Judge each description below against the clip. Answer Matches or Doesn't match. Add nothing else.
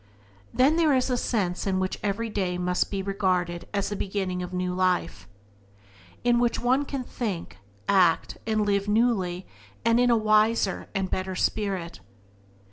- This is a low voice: Doesn't match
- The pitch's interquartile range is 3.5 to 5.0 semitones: Matches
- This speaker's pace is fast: Doesn't match